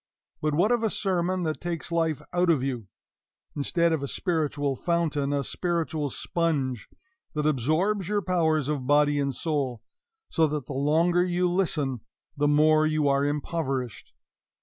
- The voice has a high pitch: No, medium, 155 Hz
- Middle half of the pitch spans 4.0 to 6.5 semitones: No, average, 3.3 semitones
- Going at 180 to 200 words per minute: No, average, 155 wpm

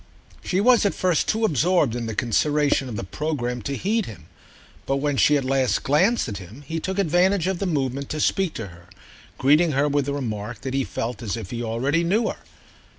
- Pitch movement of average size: No, wide, 6.3 semitones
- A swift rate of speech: Yes, fast, 215 wpm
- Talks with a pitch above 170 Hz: No, medium, 140 Hz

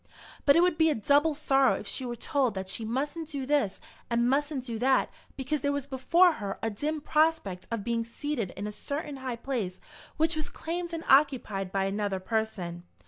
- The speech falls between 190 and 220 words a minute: Yes, average, 200 wpm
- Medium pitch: No, very high, 265 Hz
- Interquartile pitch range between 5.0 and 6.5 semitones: Yes, wide, 5.4 semitones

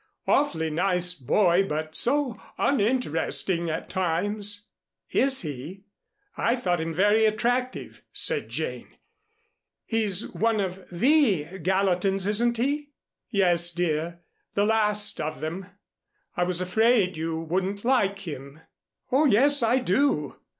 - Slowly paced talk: Yes, slow, 120 wpm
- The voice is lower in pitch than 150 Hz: No, high, 195 Hz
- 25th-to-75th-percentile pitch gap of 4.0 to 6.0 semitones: Yes, average, 5.1 semitones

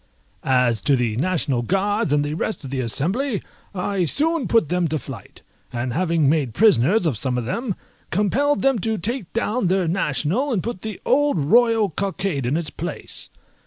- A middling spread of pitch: No, wide, 7.6 semitones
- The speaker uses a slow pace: No, average, 180 wpm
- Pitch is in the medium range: Yes, medium, 180 Hz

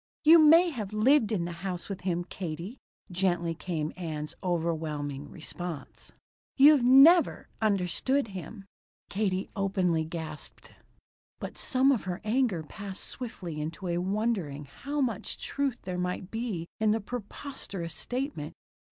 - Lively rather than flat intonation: Yes, wide, 6.2 semitones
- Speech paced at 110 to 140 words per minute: Yes, slow, 135 wpm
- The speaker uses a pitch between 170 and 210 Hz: Yes, high, 190 Hz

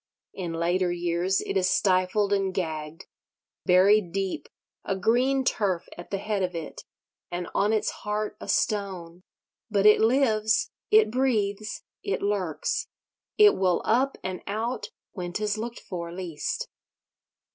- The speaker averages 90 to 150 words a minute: Yes, slow, 135 wpm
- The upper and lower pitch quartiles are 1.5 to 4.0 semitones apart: Yes, average, 3.1 semitones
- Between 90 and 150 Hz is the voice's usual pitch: No, high, 195 Hz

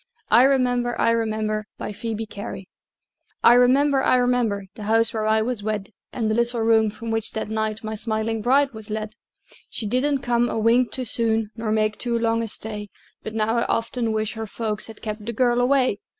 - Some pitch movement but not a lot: No, narrow, 1.9 semitones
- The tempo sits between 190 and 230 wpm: Yes, fast, 205 wpm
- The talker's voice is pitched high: Yes, high, 225 Hz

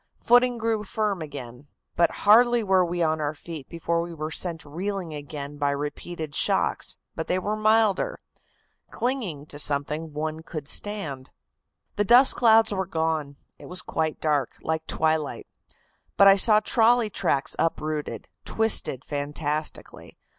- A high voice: No, medium, 165 Hz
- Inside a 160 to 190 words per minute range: No, average, 145 wpm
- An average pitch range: No, wide, 5.7 semitones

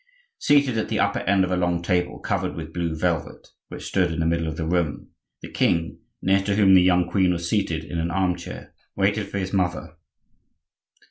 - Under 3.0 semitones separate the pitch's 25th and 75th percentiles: Yes, narrow, 2.4 semitones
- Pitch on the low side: Yes, very low, 90 Hz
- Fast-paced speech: Yes, fast, 210 wpm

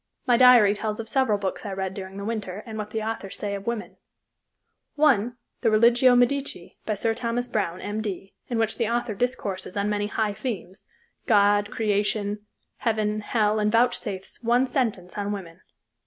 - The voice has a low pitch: No, high, 215 Hz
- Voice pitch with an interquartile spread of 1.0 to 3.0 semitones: Yes, narrow, 2.6 semitones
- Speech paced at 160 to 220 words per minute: Yes, average, 170 wpm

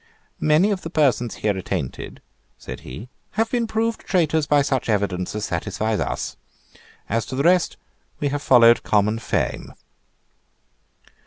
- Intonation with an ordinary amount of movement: No, wide, 7.5 semitones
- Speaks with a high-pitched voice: No, low, 130 Hz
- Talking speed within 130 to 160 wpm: Yes, average, 145 wpm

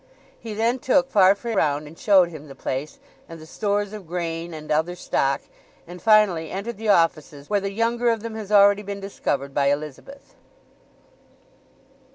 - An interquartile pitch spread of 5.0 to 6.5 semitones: Yes, average, 5.3 semitones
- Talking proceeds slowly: No, average, 170 wpm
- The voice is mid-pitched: No, high, 195 Hz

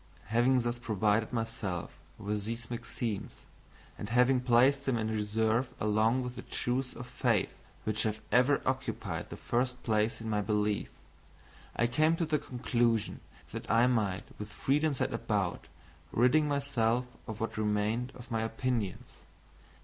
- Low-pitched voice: Yes, low, 115 Hz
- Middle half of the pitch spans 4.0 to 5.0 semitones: No, average, 2.7 semitones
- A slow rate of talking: No, average, 150 wpm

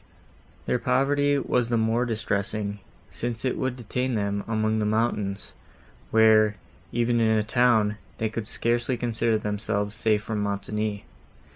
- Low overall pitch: Yes, low, 110 Hz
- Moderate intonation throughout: No, narrow, 2.2 semitones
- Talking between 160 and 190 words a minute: No, average, 140 wpm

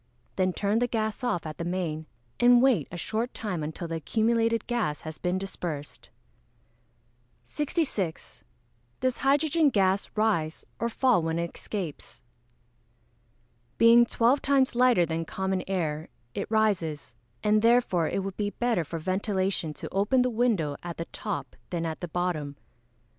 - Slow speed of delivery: No, average, 150 wpm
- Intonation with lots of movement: Yes, wide, 5.9 semitones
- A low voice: No, high, 195 Hz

